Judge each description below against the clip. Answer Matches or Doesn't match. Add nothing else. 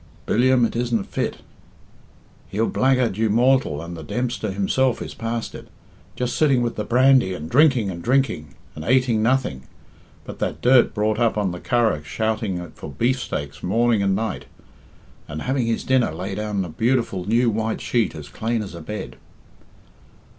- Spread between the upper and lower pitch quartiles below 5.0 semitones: Matches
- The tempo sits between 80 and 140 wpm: Doesn't match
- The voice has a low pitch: Matches